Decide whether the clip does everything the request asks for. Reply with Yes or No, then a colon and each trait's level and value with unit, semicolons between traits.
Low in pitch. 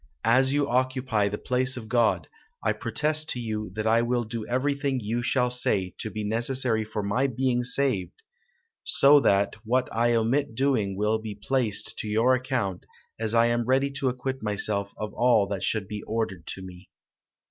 Yes: low, 115 Hz